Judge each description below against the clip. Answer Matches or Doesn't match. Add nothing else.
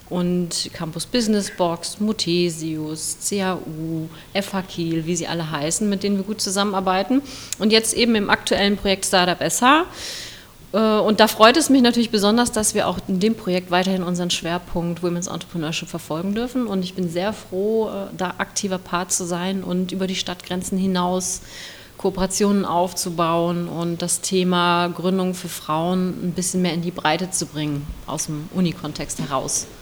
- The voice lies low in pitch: Doesn't match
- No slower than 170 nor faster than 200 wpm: Doesn't match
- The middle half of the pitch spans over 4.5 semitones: Doesn't match